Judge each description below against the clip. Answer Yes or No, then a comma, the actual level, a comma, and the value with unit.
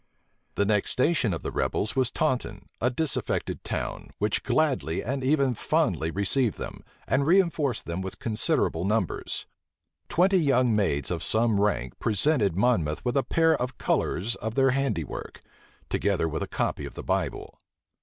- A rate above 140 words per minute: Yes, average, 155 wpm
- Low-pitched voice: Yes, low, 120 Hz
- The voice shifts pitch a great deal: Yes, wide, 5.7 semitones